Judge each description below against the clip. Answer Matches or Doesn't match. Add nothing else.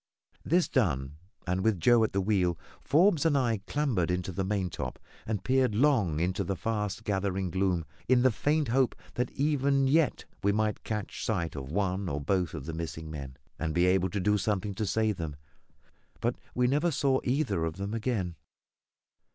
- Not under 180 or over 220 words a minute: Matches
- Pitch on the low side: Matches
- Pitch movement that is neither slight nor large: Doesn't match